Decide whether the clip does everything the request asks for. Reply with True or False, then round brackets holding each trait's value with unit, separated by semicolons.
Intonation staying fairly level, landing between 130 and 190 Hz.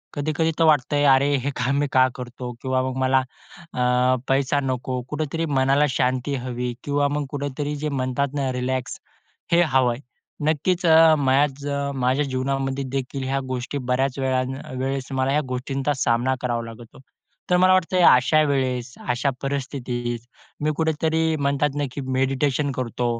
True (2.3 semitones; 135 Hz)